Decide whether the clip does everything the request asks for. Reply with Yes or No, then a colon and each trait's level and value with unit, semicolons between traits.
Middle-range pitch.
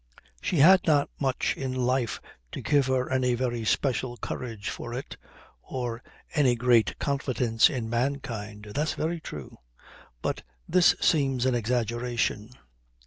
No: low, 125 Hz